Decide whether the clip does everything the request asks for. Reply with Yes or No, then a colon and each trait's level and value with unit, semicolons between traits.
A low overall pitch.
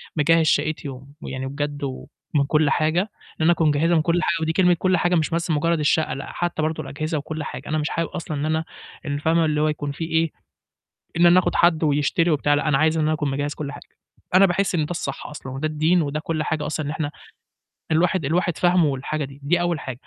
No: medium, 155 Hz